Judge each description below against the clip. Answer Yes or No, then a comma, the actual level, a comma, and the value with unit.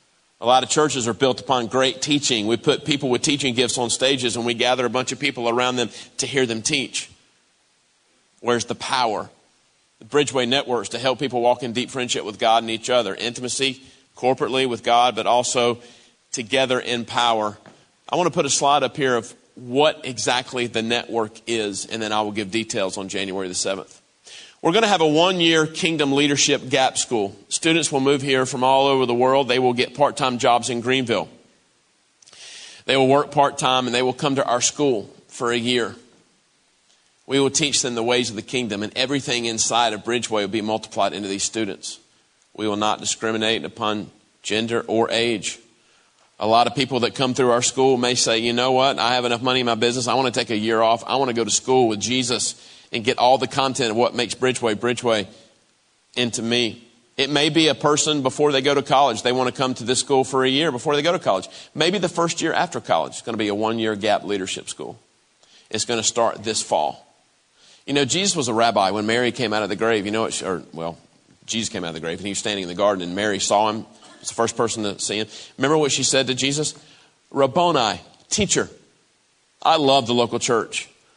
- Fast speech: Yes, fast, 225 wpm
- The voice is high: No, low, 120 Hz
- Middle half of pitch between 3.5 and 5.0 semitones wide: No, average, 2.9 semitones